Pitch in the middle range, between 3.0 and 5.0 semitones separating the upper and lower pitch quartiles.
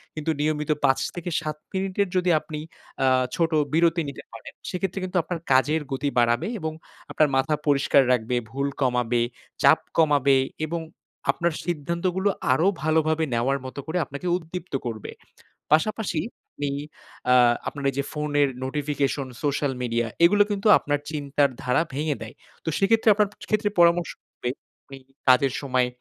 Yes: medium, 150 Hz; average, 3.9 semitones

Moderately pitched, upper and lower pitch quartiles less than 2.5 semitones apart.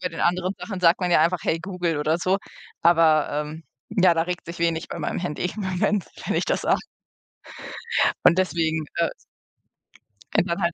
Yes: medium, 170 Hz; narrow, 1.9 semitones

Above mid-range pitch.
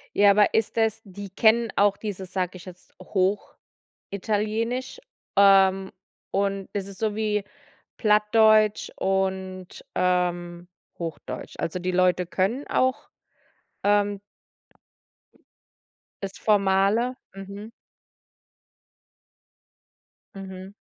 Yes: high, 195 Hz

